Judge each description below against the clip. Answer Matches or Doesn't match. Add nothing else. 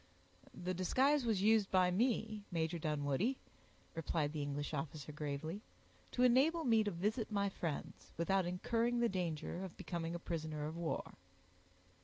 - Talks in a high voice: Doesn't match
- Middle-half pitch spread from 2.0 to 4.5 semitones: Doesn't match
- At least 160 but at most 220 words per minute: Doesn't match